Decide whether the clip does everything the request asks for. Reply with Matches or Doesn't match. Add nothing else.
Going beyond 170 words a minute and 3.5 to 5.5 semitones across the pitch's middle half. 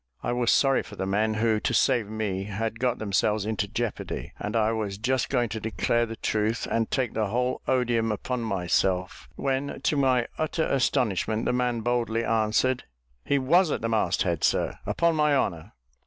Doesn't match